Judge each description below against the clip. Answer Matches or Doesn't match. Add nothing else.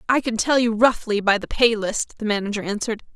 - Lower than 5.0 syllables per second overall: Doesn't match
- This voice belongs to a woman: Matches